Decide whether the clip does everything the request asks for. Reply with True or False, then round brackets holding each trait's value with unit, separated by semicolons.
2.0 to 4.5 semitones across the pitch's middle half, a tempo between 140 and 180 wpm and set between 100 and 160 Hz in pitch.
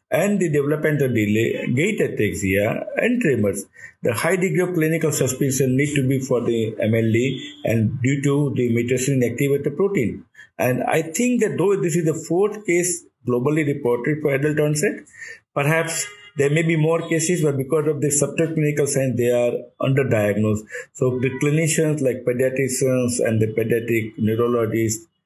False (5.0 semitones; 160 wpm; 140 Hz)